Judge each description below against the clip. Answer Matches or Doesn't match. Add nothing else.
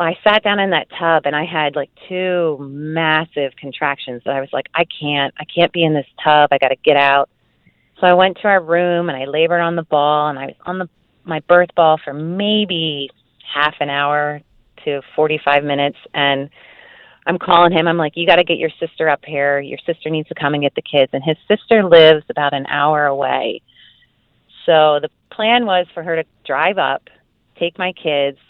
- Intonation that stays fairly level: Doesn't match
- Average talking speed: Doesn't match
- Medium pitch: Matches